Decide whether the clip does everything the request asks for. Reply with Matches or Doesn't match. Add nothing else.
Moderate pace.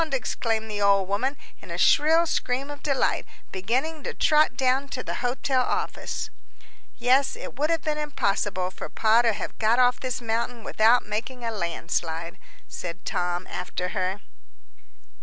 Matches